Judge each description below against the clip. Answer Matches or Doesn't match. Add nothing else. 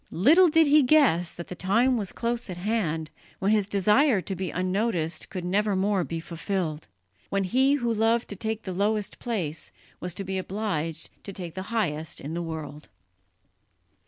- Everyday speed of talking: Matches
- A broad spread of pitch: Doesn't match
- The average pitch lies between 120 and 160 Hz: Doesn't match